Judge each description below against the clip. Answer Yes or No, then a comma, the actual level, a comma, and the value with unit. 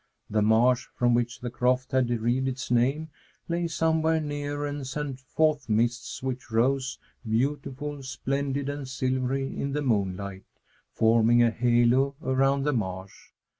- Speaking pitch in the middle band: No, low, 130 Hz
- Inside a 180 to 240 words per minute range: No, average, 140 wpm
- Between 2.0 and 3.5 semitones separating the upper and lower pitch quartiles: Yes, average, 2.9 semitones